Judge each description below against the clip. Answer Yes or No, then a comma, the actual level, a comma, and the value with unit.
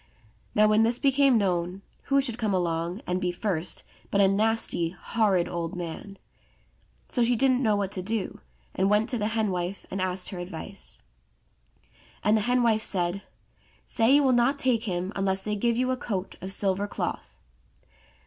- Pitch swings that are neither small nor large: Yes, average, 4.0 semitones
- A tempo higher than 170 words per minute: Yes, average, 180 wpm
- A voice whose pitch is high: Yes, high, 205 Hz